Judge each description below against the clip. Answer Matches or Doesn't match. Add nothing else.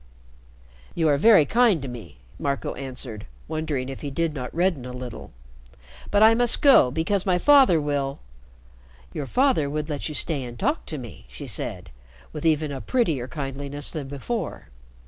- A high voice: Doesn't match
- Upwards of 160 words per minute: Matches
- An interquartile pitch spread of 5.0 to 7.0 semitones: Matches